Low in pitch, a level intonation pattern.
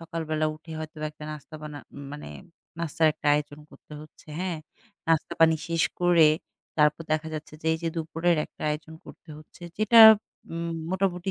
No: medium, 160 Hz; narrow, 1.6 semitones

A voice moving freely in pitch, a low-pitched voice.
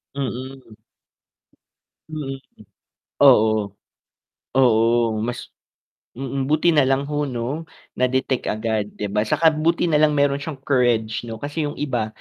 No: average, 4.1 semitones; low, 130 Hz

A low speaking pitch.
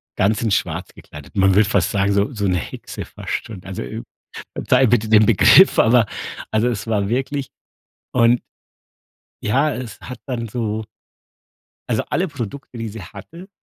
Yes: low, 110 Hz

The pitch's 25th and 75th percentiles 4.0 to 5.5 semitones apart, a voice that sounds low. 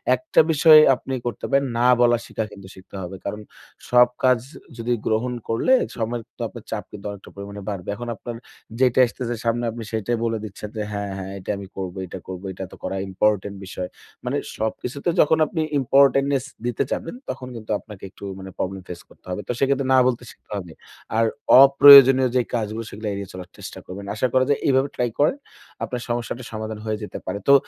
Yes: average, 4.3 semitones; low, 115 Hz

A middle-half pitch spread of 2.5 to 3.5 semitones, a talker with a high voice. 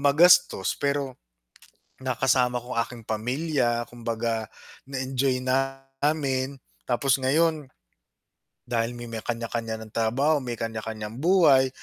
No: average, 3.0 semitones; low, 130 Hz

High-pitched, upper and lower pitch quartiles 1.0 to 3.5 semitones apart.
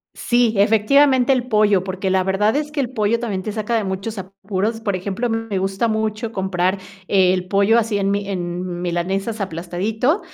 Yes: high, 205 Hz; average, 3.0 semitones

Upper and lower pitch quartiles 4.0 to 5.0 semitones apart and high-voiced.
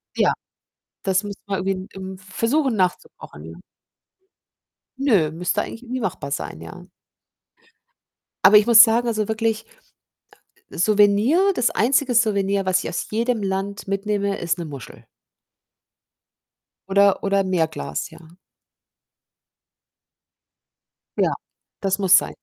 No: average, 3.1 semitones; high, 200 Hz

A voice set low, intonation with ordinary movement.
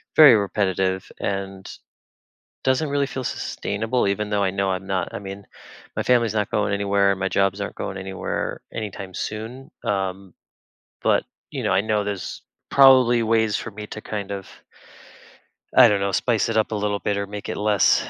No: low, 100 Hz; narrow, 2.3 semitones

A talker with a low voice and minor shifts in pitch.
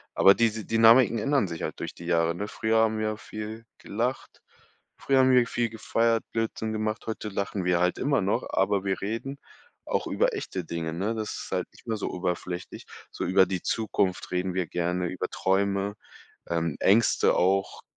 No: low, 100 Hz; average, 3.8 semitones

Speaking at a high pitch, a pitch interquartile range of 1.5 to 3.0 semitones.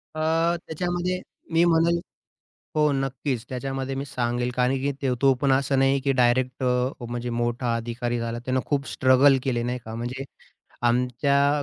No: low, 130 Hz; narrow, 2.5 semitones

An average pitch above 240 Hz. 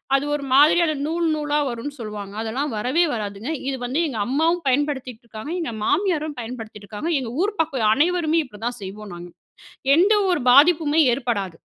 Yes: very high, 270 Hz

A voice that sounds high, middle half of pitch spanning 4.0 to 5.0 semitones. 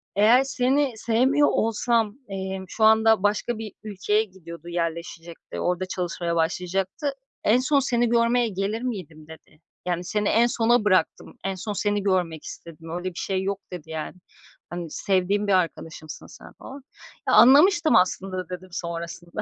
Yes: high, 195 Hz; average, 4.5 semitones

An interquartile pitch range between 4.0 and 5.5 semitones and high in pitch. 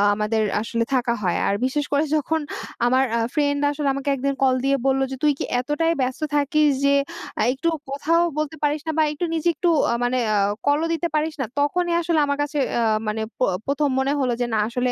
No: average, 3.0 semitones; very high, 285 Hz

